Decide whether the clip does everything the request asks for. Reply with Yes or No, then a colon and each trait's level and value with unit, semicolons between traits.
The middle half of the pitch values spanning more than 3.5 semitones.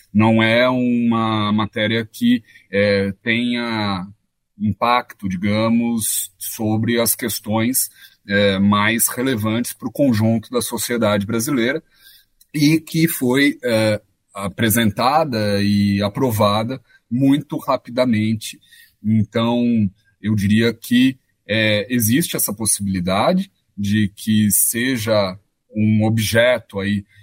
No: average, 2.7 semitones